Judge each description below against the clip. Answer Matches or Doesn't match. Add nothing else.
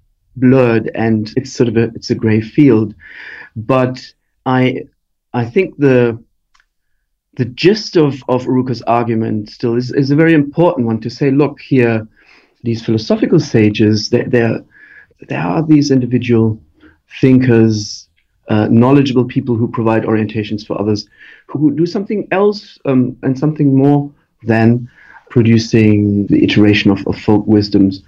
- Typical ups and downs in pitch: Matches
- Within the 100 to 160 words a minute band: Matches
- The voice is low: Matches